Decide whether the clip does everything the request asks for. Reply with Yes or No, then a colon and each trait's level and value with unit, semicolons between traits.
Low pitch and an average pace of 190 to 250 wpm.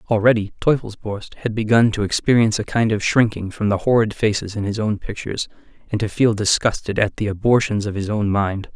Yes: low, 105 Hz; average, 200 wpm